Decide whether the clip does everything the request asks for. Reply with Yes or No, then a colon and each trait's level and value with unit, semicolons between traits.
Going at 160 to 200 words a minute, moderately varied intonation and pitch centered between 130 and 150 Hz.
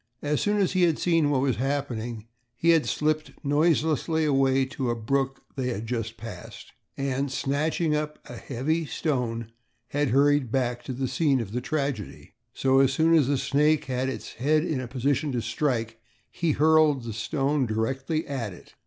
Yes: average, 180 wpm; average, 3.7 semitones; low, 135 Hz